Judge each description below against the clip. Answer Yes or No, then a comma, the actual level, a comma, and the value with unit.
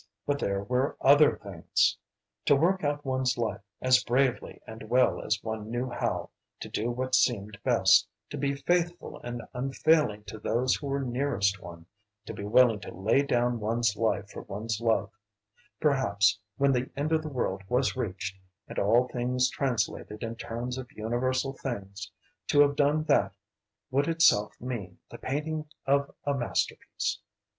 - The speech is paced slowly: No, average, 165 wpm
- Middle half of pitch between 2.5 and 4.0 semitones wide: No, average, 4.4 semitones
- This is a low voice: Yes, low, 125 Hz